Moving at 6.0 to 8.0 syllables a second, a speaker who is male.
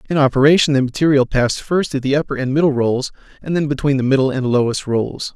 Yes: 6.4 syllables/s; male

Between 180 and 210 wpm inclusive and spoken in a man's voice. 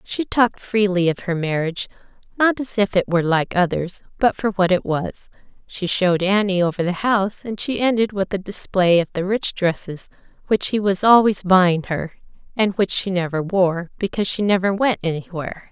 No: average, 190 wpm; female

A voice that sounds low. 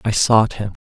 Yes: low, 110 Hz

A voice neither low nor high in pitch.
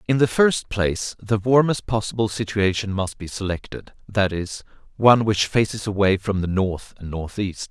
No: low, 105 Hz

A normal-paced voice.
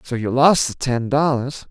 No: fast, 210 wpm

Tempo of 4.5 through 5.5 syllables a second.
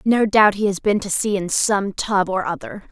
Yes: 4.7 syllables/s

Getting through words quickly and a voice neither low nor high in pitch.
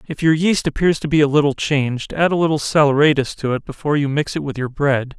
Yes: fast, 255 wpm; medium, 145 Hz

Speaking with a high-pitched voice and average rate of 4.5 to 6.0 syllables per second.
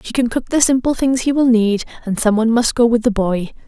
Yes: high, 235 Hz; 5.8 syllables/s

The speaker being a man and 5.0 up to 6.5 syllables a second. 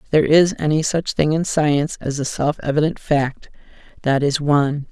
No: female; 5.2 syllables/s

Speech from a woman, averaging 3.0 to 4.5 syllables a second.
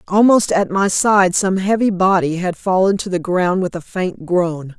Yes: female; 4.3 syllables/s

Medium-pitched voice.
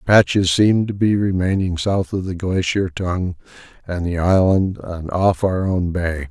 No: very low, 90 Hz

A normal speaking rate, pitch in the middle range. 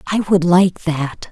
Yes: average, 185 wpm; medium, 175 Hz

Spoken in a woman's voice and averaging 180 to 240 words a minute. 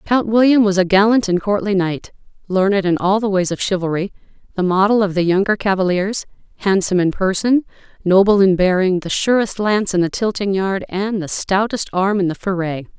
Yes: female; average, 190 wpm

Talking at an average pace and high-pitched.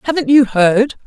Yes: average, 170 wpm; high, 245 Hz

